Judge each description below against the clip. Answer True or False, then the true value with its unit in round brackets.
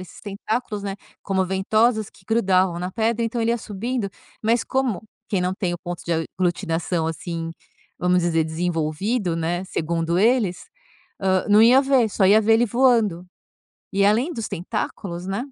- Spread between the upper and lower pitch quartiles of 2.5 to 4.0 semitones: False (4.4 semitones)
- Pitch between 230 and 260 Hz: False (195 Hz)